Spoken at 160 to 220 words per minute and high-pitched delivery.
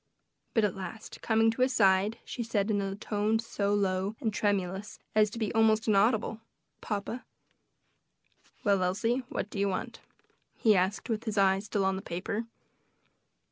Yes: average, 165 wpm; high, 210 Hz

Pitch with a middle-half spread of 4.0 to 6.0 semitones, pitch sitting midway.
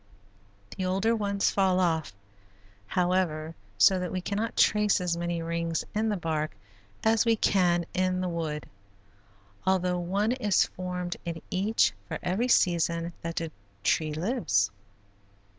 No: average, 2.9 semitones; medium, 180 Hz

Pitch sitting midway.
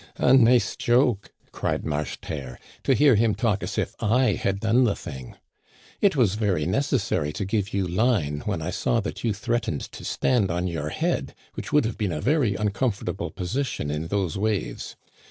No: low, 105 Hz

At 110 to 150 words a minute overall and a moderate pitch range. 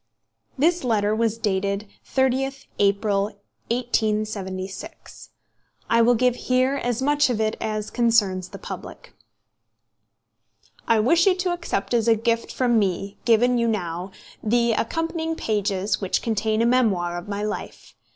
Yes: average, 140 wpm; average, 3.5 semitones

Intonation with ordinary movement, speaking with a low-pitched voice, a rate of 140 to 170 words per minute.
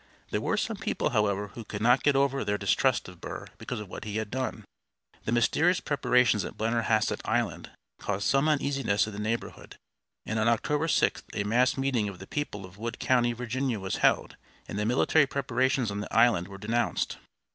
No: average, 4.0 semitones; low, 115 Hz; average, 195 wpm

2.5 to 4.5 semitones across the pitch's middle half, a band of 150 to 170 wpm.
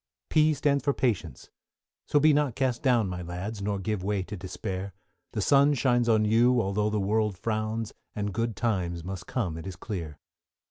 No: average, 4.2 semitones; average, 185 wpm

